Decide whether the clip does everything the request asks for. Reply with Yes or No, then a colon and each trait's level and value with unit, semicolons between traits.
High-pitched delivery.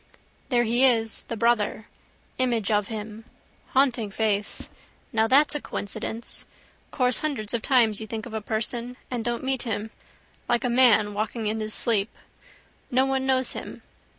Yes: high, 230 Hz